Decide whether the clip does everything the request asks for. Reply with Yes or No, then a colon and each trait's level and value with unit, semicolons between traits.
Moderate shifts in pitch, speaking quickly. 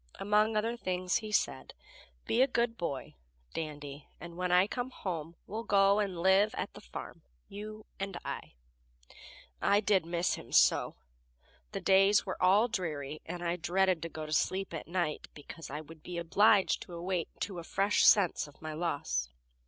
No: average, 3.7 semitones; average, 175 wpm